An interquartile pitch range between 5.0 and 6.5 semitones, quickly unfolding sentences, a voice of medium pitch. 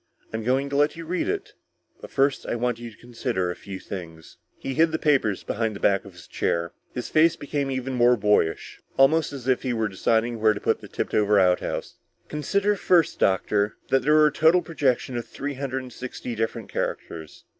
No: wide, 5.6 semitones; fast, 215 wpm; low, 125 Hz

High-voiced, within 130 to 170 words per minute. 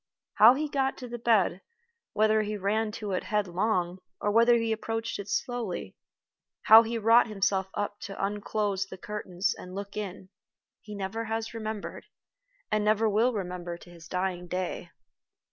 Yes: high, 210 Hz; average, 160 wpm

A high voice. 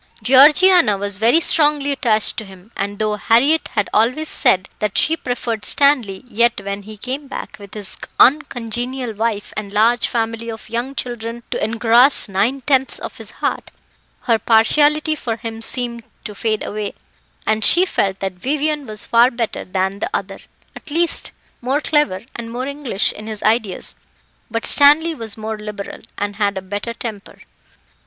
Yes: high, 230 Hz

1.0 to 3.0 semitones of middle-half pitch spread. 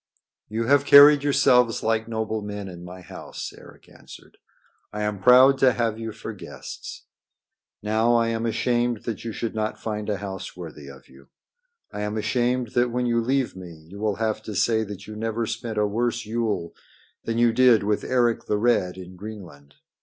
Yes: narrow, 2.6 semitones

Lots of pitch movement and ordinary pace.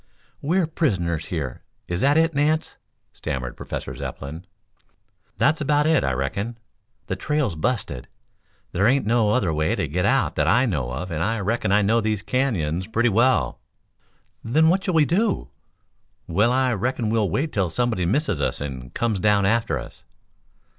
Yes: wide, 7.7 semitones; average, 170 wpm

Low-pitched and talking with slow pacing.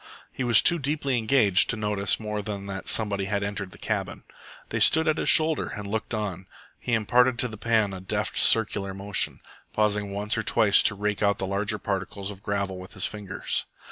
No: low, 105 Hz; fast, 205 wpm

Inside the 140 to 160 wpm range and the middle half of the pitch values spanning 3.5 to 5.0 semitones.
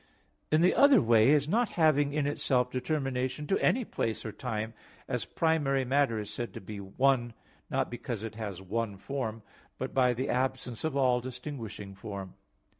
No: average, 175 wpm; average, 4.1 semitones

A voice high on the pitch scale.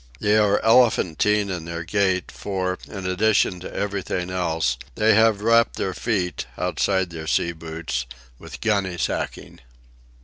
No: very low, 95 Hz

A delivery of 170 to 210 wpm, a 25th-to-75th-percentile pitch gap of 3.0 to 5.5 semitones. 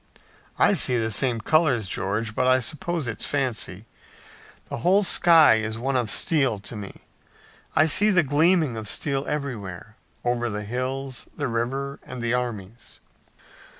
No: average, 150 wpm; average, 4.4 semitones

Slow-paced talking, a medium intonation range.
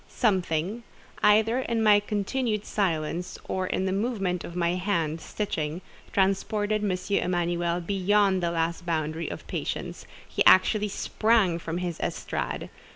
Yes: slow, 125 wpm; average, 3.5 semitones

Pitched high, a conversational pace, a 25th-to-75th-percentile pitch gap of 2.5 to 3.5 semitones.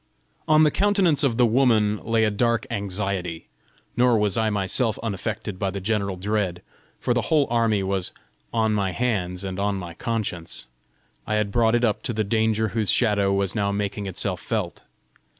No: low, 105 Hz; average, 180 wpm; average, 2.9 semitones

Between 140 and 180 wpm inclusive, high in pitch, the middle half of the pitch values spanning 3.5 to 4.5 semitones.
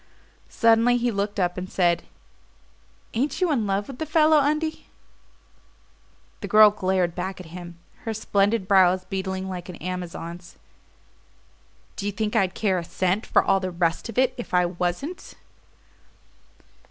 Yes: average, 155 wpm; high, 195 Hz; average, 4.2 semitones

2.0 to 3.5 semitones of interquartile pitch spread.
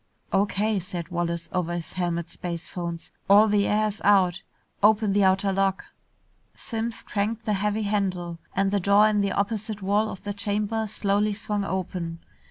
Yes: narrow, 2.4 semitones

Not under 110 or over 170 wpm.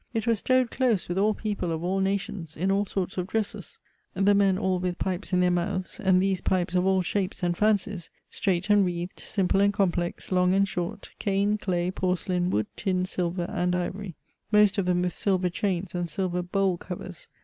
No: average, 200 wpm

